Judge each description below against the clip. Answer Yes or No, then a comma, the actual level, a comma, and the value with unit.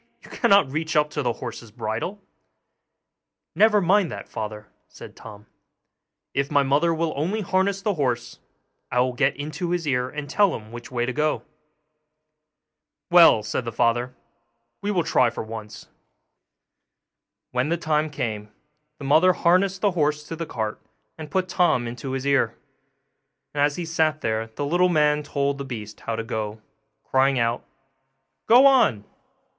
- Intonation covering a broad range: Yes, wide, 6.1 semitones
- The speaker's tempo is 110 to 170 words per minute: Yes, average, 160 wpm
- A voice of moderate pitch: Yes, medium, 145 Hz